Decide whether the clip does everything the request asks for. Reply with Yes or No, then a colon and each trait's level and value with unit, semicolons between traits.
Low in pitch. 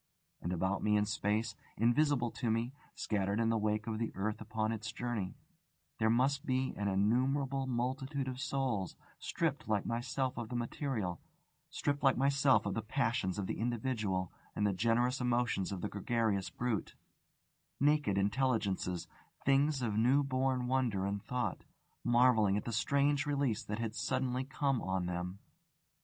Yes: low, 115 Hz